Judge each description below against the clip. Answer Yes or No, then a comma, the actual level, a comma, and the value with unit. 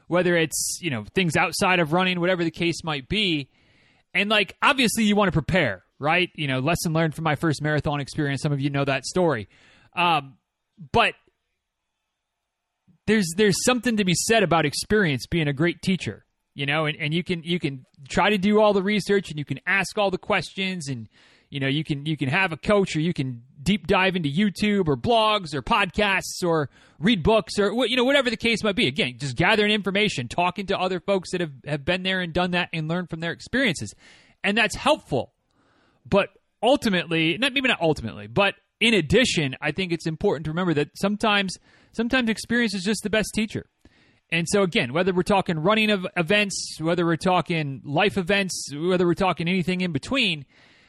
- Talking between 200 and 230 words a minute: Yes, fast, 205 wpm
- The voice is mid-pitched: Yes, medium, 180 Hz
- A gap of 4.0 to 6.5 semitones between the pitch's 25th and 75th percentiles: Yes, average, 4.7 semitones